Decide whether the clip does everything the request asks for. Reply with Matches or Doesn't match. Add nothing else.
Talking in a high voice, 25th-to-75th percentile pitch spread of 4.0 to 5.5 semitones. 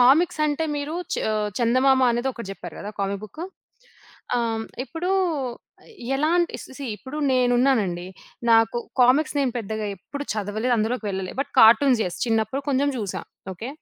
Matches